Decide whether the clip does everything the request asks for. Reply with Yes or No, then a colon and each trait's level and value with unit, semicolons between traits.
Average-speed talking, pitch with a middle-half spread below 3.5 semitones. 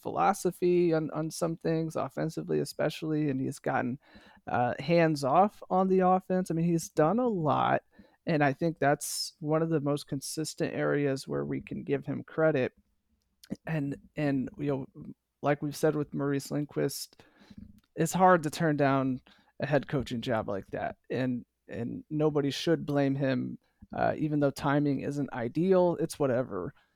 Yes: average, 160 wpm; average, 2.9 semitones